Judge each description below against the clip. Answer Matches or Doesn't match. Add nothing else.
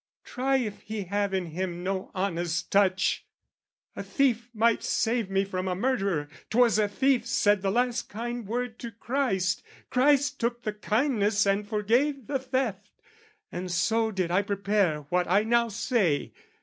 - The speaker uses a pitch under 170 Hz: Doesn't match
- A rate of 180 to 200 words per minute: Doesn't match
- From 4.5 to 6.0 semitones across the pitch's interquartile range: Doesn't match